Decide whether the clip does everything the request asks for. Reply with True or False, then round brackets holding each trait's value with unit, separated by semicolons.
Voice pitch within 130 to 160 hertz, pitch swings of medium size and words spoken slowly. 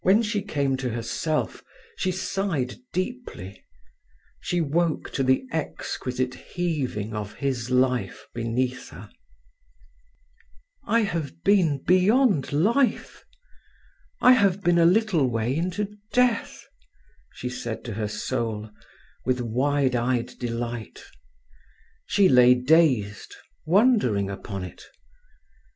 False (135 Hz; 7.4 semitones; 110 wpm)